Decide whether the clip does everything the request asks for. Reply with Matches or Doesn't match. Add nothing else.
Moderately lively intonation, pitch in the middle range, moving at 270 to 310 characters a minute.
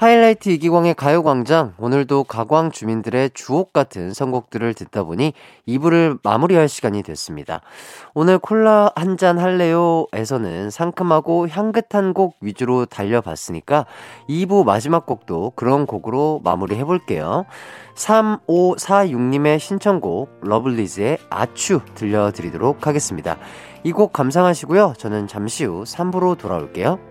Doesn't match